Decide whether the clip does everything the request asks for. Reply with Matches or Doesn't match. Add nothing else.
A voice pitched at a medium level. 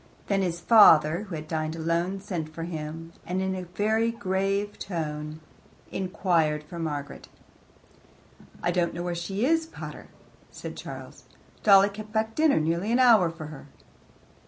Matches